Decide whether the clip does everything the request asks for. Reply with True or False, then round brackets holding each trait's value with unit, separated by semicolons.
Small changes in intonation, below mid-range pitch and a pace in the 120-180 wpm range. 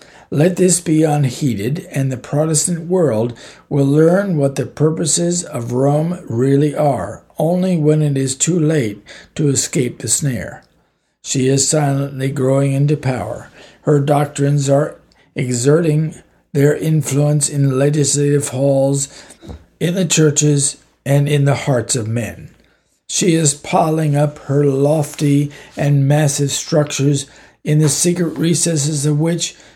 False (2.2 semitones; 145 Hz; 135 wpm)